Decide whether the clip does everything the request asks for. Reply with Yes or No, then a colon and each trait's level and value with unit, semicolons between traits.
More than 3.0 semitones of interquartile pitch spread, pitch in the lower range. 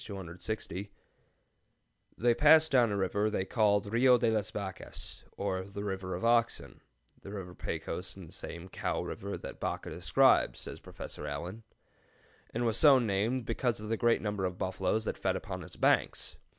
Yes: average, 3.6 semitones; low, 105 Hz